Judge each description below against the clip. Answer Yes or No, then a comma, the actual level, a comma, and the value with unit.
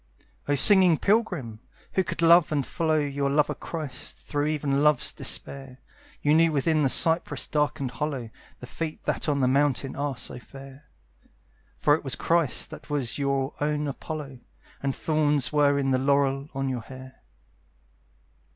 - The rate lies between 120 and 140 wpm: No, average, 160 wpm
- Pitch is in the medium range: Yes, medium, 145 Hz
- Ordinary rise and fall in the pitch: No, narrow, 2.2 semitones